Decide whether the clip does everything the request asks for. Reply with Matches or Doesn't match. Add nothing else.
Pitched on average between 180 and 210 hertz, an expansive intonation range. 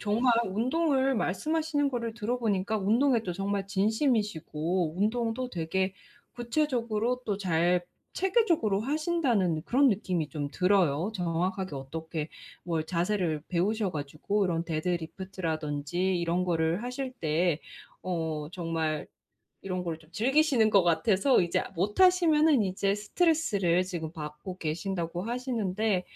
Matches